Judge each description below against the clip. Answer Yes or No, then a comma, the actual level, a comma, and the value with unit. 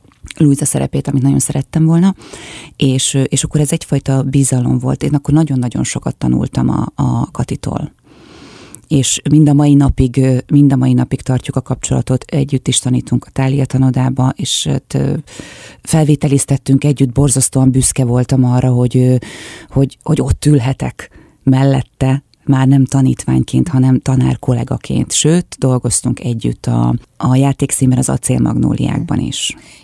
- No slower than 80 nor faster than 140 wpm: Yes, average, 135 wpm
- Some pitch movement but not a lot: No, narrow, 2.0 semitones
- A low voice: Yes, low, 130 Hz